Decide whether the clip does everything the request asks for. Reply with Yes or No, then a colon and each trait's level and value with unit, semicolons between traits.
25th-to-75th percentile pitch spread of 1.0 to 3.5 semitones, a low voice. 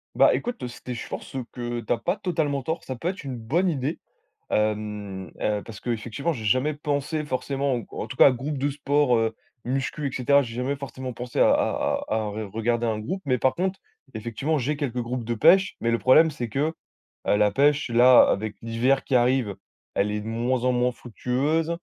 No: average, 3.9 semitones; low, 125 Hz